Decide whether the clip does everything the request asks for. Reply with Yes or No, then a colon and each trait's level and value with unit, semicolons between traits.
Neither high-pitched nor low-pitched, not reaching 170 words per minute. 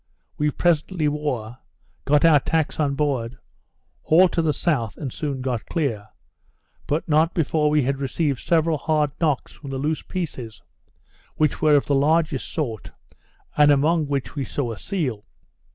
Yes: medium, 150 Hz; average, 160 wpm